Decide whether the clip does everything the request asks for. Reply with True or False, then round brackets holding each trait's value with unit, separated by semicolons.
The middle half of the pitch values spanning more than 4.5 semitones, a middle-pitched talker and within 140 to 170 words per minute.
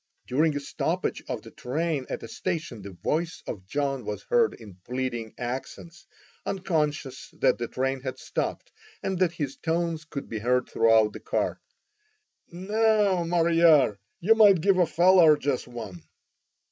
True (5.5 semitones; 150 Hz; 155 wpm)